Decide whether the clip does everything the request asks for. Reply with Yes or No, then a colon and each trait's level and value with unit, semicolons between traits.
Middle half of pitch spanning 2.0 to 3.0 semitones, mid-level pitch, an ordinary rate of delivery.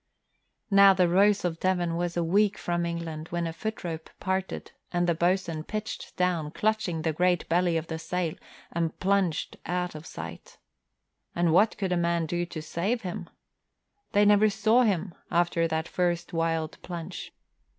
Yes: narrow, 2.4 semitones; medium, 175 Hz; average, 170 wpm